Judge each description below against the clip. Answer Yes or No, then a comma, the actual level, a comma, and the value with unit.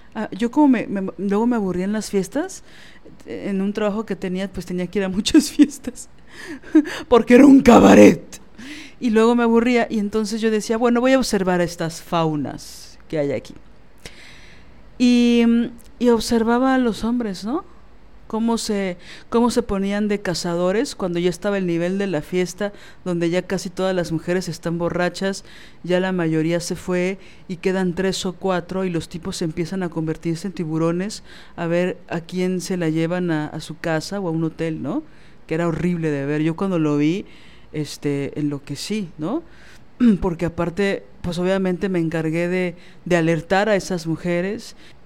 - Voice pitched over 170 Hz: Yes, medium, 185 Hz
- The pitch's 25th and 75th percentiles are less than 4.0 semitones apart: No, average, 4.5 semitones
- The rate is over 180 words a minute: No, average, 175 wpm